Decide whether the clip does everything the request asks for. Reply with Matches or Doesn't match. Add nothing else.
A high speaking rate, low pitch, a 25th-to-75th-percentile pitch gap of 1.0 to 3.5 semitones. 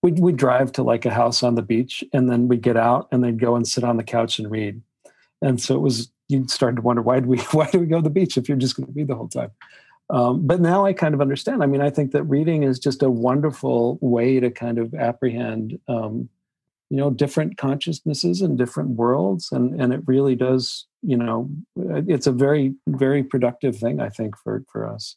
Matches